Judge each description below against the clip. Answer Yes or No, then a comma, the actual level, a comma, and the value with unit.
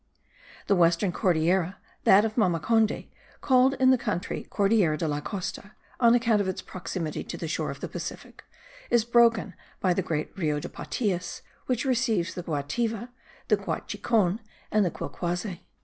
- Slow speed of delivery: No, average, 160 wpm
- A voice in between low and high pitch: No, high, 200 Hz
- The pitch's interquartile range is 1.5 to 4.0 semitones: No, average, 4.8 semitones